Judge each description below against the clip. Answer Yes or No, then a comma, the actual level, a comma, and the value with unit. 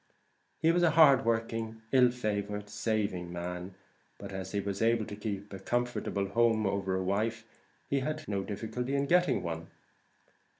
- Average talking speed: Yes, average, 165 wpm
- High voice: No, low, 110 Hz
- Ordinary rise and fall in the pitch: Yes, average, 3.8 semitones